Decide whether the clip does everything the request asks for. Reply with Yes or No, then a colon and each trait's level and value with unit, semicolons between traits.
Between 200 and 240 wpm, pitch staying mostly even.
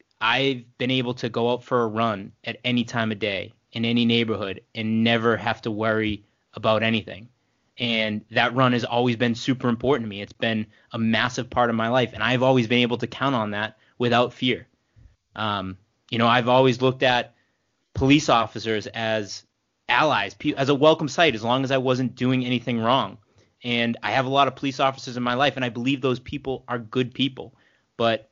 Yes: fast, 205 wpm; narrow, 2.3 semitones